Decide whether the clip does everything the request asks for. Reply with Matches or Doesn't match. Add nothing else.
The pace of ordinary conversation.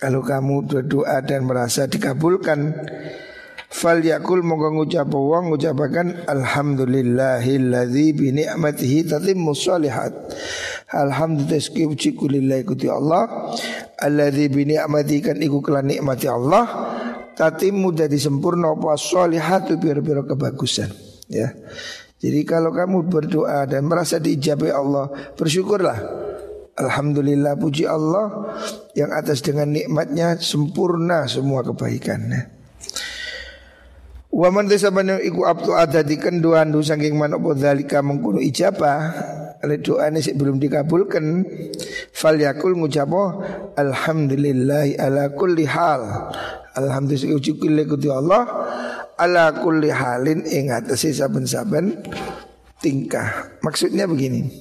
Matches